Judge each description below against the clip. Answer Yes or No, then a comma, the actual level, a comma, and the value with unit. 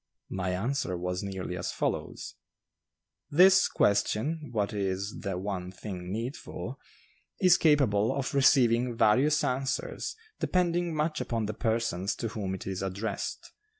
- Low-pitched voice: Yes, low, 110 Hz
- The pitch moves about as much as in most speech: No, wide, 6.4 semitones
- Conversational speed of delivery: No, slow, 130 wpm